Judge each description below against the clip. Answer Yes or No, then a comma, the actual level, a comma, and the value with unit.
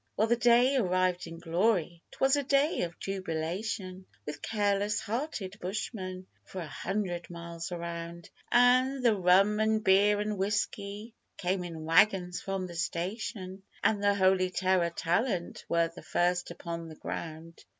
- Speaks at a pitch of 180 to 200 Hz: Yes, high, 190 Hz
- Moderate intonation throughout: Yes, average, 3.6 semitones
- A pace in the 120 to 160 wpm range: Yes, average, 150 wpm